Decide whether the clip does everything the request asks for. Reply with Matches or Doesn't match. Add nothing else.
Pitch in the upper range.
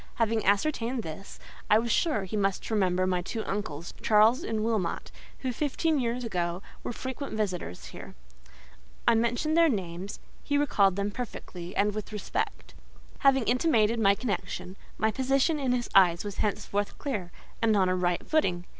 Matches